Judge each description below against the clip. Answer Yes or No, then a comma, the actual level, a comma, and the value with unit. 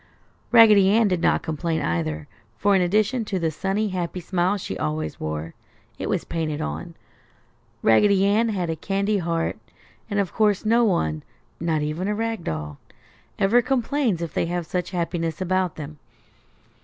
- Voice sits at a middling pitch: Yes, medium, 180 Hz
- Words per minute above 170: No, average, 165 wpm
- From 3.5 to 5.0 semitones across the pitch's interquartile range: Yes, average, 4.7 semitones